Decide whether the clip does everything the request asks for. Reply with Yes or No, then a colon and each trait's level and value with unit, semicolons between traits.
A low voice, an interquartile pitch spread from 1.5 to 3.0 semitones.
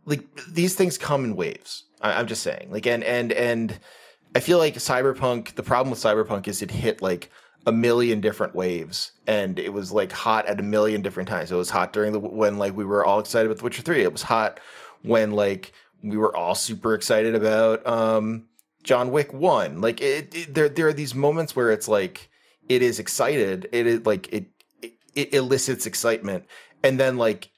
No: low, 115 Hz; average, 3.8 semitones